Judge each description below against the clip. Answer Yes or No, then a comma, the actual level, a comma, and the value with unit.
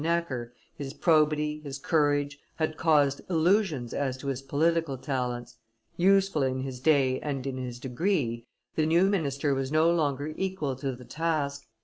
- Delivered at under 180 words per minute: Yes, average, 155 wpm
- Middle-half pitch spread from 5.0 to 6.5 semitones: No, average, 3.4 semitones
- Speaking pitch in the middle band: Yes, medium, 145 Hz